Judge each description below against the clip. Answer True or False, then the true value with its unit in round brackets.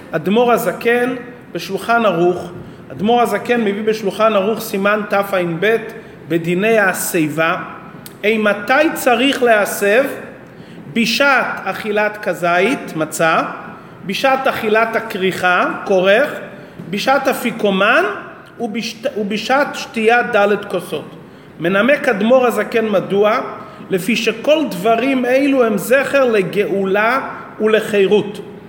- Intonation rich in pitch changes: False (3.6 semitones)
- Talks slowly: True (90 wpm)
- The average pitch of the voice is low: False (210 Hz)